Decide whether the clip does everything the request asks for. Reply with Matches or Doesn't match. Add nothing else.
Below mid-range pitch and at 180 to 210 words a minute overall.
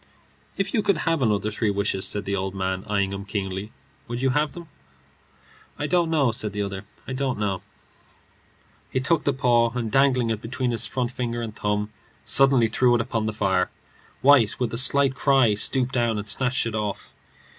Matches